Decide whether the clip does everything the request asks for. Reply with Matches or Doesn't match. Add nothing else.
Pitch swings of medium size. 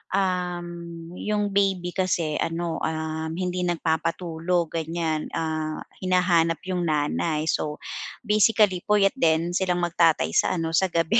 Doesn't match